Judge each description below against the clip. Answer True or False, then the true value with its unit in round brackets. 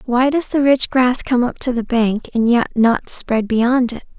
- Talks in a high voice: True (245 Hz)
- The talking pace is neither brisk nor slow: False (230 wpm)